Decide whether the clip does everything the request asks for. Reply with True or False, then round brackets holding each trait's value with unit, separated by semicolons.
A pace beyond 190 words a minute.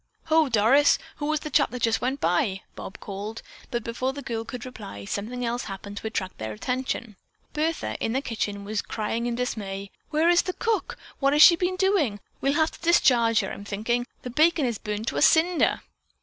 True (205 wpm)